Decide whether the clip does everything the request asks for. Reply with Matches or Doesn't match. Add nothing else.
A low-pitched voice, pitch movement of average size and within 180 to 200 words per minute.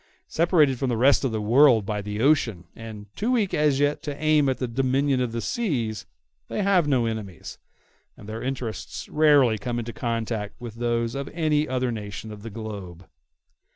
Matches